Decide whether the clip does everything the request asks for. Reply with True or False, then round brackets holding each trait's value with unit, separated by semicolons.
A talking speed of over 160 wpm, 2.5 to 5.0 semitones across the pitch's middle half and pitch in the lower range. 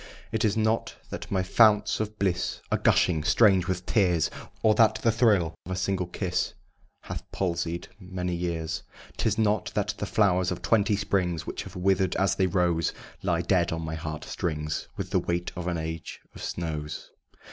True (180 wpm; 3.3 semitones; 90 Hz)